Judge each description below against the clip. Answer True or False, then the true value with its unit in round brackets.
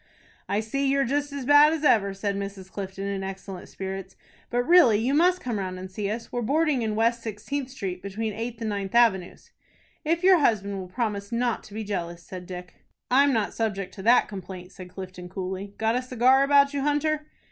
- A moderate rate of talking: False (210 wpm)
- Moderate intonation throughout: False (5.7 semitones)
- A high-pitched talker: True (220 Hz)